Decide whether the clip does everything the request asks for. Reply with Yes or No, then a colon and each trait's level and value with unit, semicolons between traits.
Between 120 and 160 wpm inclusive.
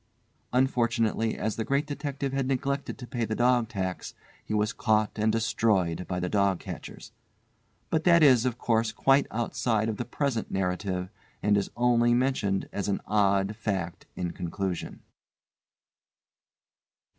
Yes: average, 145 wpm